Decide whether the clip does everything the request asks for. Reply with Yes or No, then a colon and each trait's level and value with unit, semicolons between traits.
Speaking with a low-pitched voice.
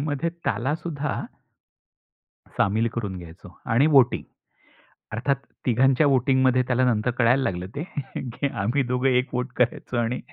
Yes: low, 125 Hz